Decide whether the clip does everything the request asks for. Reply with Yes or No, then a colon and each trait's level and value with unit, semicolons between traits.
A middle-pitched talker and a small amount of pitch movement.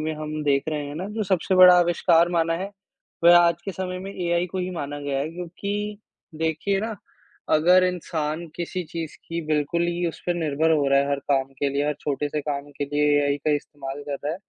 No: medium, 160 Hz; average, 3.4 semitones